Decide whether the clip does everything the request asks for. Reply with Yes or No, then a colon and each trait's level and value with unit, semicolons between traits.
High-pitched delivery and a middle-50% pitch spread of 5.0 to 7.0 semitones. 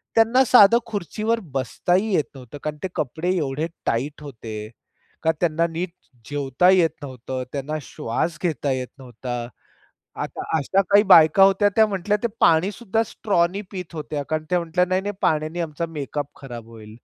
No: medium, 160 Hz; wide, 5.6 semitones